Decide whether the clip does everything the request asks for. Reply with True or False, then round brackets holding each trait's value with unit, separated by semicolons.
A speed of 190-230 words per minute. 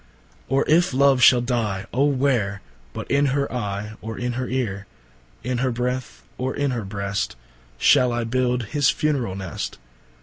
False (145 wpm)